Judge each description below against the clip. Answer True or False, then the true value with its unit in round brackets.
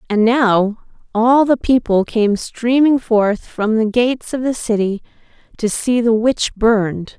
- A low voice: False (230 Hz)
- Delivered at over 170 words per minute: False (160 wpm)